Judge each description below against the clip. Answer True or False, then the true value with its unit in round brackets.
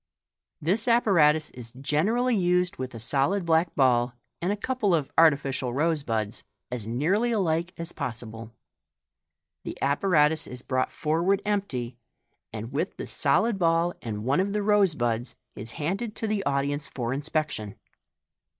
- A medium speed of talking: True (150 wpm)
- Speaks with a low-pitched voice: False (155 Hz)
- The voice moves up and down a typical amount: False (7.2 semitones)